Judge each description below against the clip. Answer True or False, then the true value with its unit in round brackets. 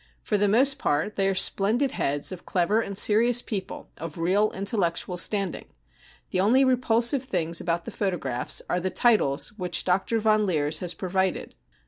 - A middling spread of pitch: True (4.1 semitones)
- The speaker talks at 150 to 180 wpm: True (165 wpm)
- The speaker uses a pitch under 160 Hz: False (195 Hz)